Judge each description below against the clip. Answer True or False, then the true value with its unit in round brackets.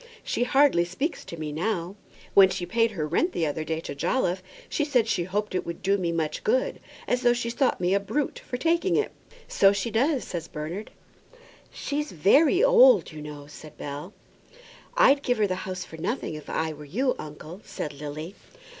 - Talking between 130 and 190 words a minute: False (200 wpm)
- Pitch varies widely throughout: True (8.0 semitones)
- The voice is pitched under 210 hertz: True (190 Hz)